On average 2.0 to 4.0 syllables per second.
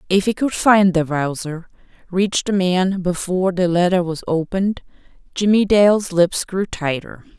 No: 4.6 syllables/s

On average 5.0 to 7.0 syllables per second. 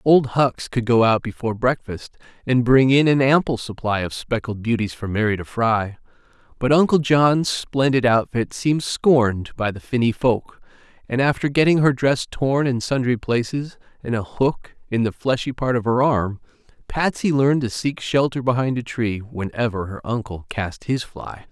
No: 4.8 syllables/s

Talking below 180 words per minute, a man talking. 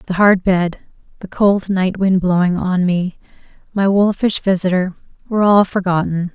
No: average, 150 wpm; female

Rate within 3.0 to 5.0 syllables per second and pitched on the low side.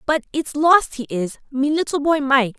No: 4.6 syllables/s; very high, 280 Hz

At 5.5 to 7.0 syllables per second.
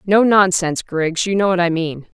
No: 5.1 syllables/s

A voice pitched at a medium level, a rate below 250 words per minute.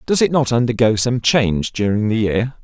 No: low, 115 Hz; fast, 205 wpm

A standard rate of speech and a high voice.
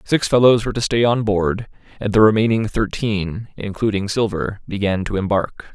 No: average, 165 wpm; low, 105 Hz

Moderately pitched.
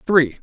Yes: medium, 155 Hz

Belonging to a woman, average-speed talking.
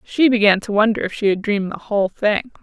No: female; fast, 250 wpm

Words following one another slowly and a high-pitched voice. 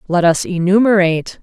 No: slow, 125 wpm; medium, 180 Hz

